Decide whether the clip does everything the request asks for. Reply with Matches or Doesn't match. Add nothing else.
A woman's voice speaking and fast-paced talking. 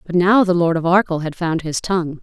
Matches